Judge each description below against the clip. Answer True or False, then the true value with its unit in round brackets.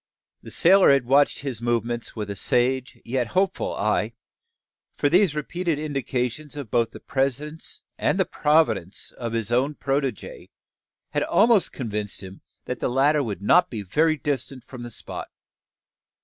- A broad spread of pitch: False (4.3 semitones)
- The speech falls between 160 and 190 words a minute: False (150 wpm)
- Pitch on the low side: True (130 Hz)